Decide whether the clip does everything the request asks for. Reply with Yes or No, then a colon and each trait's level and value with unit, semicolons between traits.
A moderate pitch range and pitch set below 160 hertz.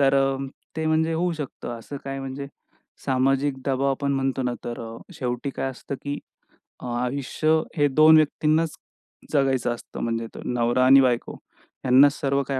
No: narrow, 2.1 semitones; low, 135 Hz